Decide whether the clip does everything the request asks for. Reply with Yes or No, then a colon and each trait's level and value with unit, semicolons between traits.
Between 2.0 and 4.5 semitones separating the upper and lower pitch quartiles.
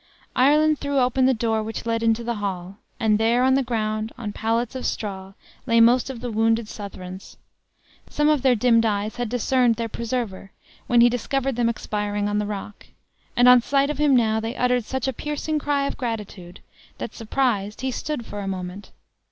Yes: average, 3.4 semitones